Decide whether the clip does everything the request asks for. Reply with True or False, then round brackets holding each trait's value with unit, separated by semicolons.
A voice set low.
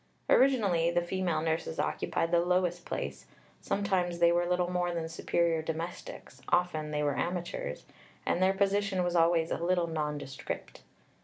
False (175 Hz)